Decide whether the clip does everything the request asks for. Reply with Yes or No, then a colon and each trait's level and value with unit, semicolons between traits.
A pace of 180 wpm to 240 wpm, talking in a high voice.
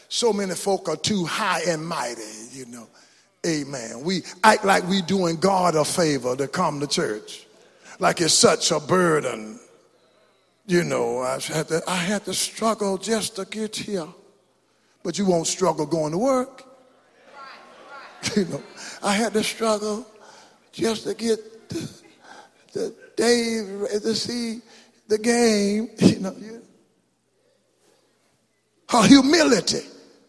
No: slow, 135 wpm; high, 195 Hz